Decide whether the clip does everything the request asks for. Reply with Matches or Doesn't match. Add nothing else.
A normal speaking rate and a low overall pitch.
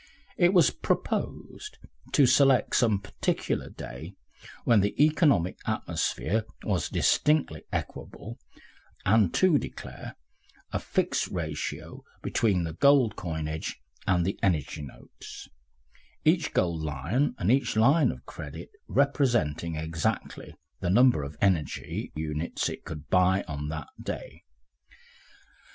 Doesn't match